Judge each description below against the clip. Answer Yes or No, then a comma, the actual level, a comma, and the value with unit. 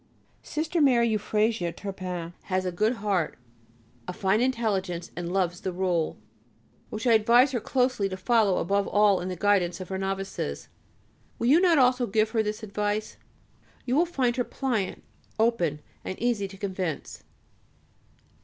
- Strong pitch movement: No, average, 4.2 semitones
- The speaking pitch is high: Yes, high, 205 Hz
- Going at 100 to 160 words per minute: Yes, average, 155 wpm